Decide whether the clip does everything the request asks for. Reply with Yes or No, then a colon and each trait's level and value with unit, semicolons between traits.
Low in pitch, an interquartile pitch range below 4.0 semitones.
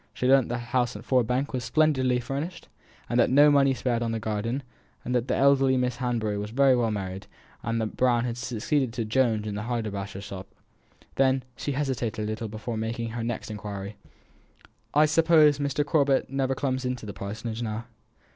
Yes: low, 120 Hz; average, 3.5 semitones